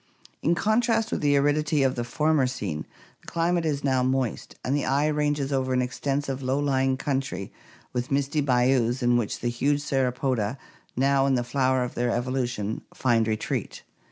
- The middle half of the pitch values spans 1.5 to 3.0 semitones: Yes, average, 2.7 semitones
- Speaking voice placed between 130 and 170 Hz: Yes, low, 135 Hz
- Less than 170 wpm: No, average, 175 wpm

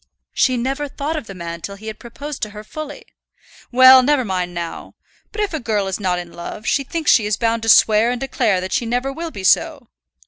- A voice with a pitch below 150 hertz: No, high, 230 Hz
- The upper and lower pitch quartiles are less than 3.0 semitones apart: No, wide, 5.4 semitones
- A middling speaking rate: No, fast, 235 wpm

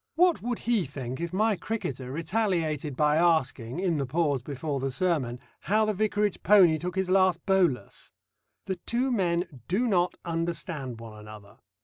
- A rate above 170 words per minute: No, average, 160 wpm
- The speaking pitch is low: No, medium, 170 Hz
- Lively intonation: Yes, wide, 5.9 semitones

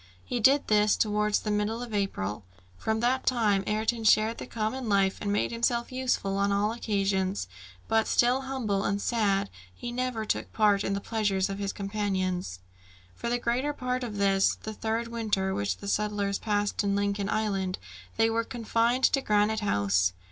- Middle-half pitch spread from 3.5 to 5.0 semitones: No, average, 2.7 semitones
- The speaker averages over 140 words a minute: Yes, average, 175 wpm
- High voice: Yes, high, 210 Hz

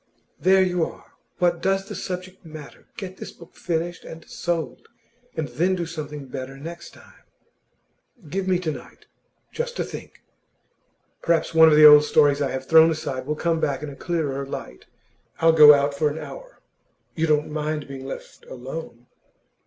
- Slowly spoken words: No, average, 175 wpm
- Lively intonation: No, average, 3.2 semitones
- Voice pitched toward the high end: No, medium, 160 Hz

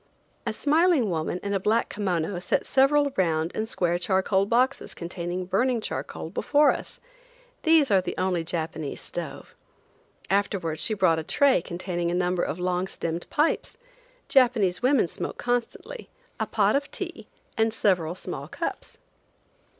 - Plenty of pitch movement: Yes, wide, 6.9 semitones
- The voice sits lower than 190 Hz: No, high, 195 Hz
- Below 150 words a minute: Yes, average, 140 wpm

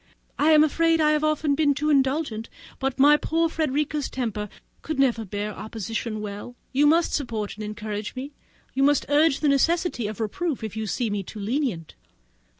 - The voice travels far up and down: Yes, wide, 5.8 semitones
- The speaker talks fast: No, average, 180 wpm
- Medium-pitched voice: No, very high, 270 Hz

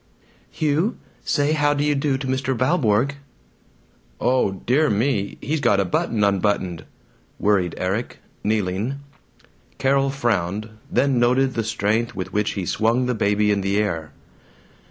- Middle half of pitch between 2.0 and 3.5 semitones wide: No, average, 5.1 semitones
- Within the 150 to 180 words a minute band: No, average, 140 wpm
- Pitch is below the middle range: Yes, low, 115 Hz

